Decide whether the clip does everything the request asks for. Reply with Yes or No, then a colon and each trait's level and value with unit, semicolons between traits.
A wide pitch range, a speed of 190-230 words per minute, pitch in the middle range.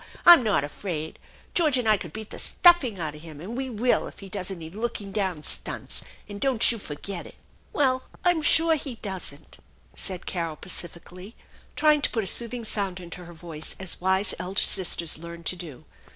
No: wide, 5.7 semitones; average, 200 wpm; high, 195 Hz